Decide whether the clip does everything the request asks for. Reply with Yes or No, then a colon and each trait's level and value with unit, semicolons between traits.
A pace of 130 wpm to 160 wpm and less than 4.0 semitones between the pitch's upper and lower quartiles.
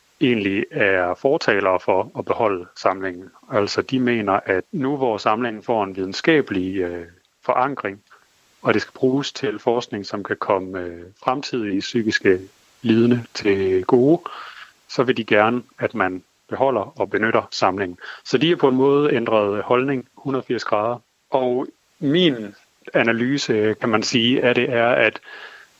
No: average, 150 wpm; average, 4.4 semitones